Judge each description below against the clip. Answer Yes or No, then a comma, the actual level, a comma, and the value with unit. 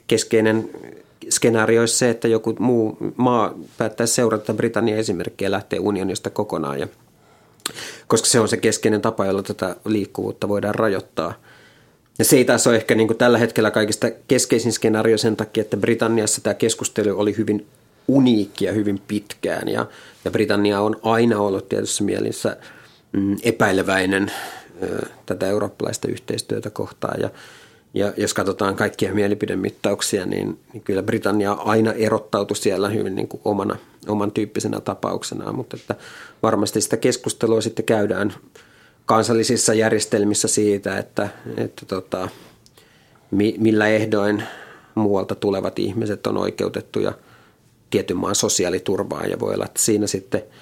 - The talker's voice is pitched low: Yes, low, 110 Hz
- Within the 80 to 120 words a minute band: No, average, 130 wpm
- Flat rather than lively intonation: Yes, narrow, 1.6 semitones